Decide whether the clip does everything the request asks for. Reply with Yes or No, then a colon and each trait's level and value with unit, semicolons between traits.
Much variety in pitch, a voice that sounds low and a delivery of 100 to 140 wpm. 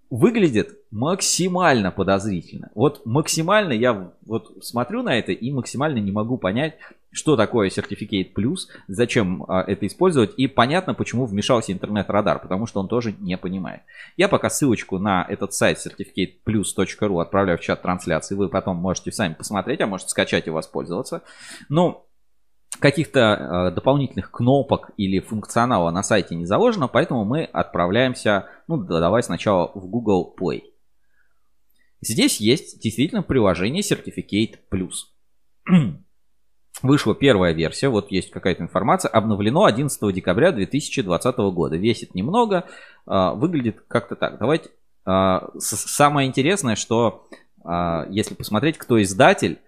Yes: wide, 5.8 semitones; low, 105 Hz; average, 130 wpm